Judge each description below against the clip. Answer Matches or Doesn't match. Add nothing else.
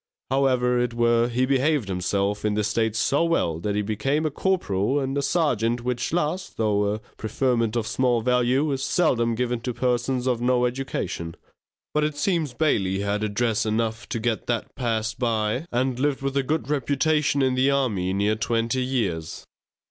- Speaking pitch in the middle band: Doesn't match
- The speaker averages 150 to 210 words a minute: Matches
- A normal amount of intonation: Matches